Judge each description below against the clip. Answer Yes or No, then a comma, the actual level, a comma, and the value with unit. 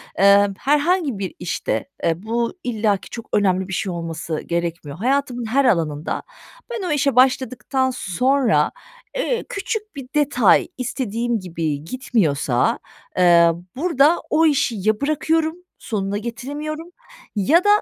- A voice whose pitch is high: Yes, high, 235 Hz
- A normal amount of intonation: No, wide, 7.2 semitones